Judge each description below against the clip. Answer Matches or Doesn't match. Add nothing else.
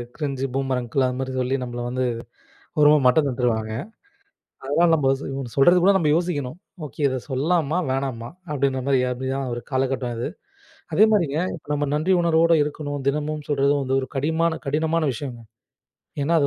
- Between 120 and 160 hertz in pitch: Matches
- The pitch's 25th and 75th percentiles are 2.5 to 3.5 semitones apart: Matches